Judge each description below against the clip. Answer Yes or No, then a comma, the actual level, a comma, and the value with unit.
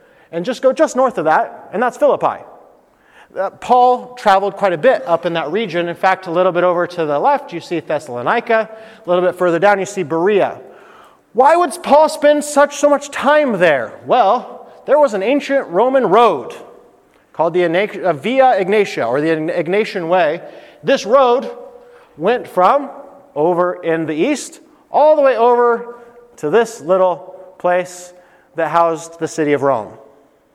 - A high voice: Yes, high, 200 Hz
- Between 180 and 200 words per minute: No, average, 165 wpm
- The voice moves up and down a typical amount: No, wide, 7.2 semitones